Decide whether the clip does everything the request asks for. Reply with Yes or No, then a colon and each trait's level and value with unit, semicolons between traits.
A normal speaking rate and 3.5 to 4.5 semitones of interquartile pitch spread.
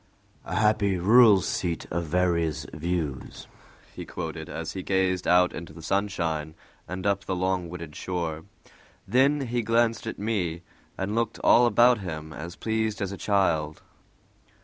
Yes: average, 150 wpm; average, 4.2 semitones